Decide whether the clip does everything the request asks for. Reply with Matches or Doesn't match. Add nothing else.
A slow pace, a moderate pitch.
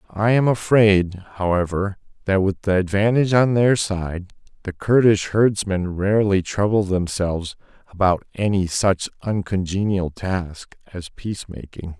Doesn't match